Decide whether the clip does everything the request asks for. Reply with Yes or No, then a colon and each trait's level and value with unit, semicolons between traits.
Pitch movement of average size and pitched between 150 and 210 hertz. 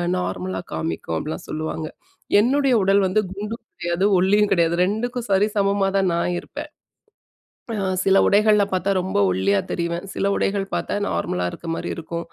Yes: average, 3.5 semitones; high, 190 Hz